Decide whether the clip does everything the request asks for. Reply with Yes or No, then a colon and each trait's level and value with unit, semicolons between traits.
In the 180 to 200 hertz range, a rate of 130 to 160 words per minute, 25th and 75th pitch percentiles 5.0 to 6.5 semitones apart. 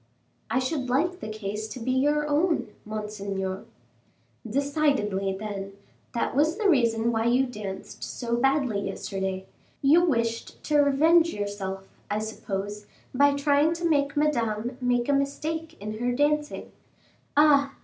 No: very high, 250 Hz; average, 140 wpm; wide, 5.6 semitones